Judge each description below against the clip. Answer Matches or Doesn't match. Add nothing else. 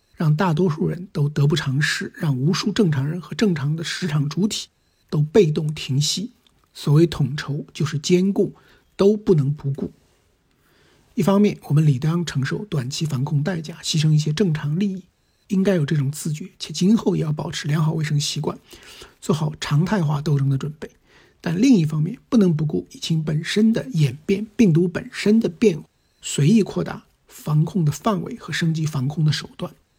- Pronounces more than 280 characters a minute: Doesn't match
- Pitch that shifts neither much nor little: Matches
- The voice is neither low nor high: Matches